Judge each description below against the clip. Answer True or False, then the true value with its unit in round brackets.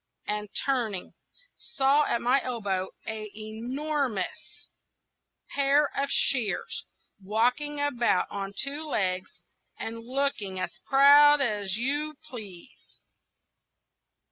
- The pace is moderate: False (95 wpm)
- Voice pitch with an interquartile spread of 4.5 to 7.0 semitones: True (5.2 semitones)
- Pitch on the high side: True (245 Hz)